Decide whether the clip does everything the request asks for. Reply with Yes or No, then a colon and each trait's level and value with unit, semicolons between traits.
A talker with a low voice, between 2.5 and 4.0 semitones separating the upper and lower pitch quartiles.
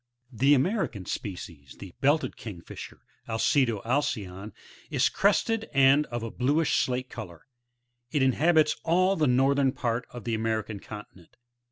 No: low, 125 Hz; average, 5.2 semitones